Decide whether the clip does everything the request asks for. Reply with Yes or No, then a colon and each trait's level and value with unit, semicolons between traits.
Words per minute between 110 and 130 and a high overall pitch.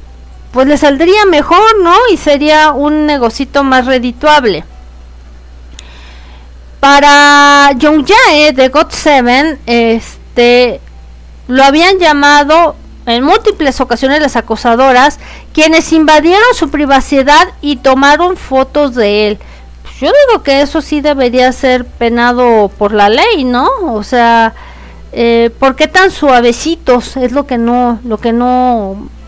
Yes: slow, 125 wpm; very high, 265 Hz